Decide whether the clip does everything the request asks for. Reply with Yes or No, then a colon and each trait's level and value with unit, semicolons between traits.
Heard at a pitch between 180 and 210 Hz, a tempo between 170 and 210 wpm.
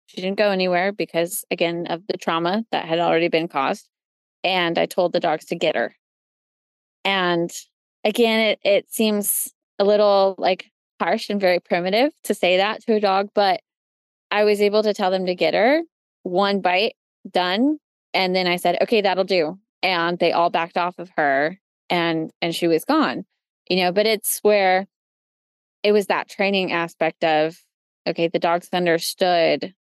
Yes: medium, 185 Hz; average, 175 wpm